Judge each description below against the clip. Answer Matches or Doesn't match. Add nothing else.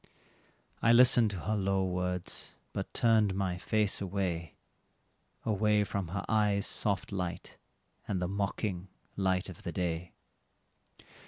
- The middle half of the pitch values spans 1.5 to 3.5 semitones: Matches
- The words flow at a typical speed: Doesn't match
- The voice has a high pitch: Doesn't match